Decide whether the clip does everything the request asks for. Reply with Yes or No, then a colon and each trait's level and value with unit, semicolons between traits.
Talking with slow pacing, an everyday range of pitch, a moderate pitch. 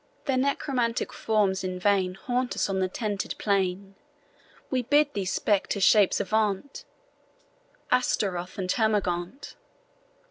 No: slow, 115 wpm; average, 4.6 semitones; high, 205 Hz